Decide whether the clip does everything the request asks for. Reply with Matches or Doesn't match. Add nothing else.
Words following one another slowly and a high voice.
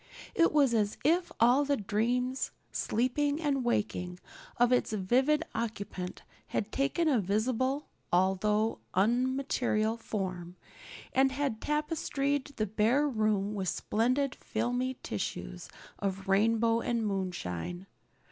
Matches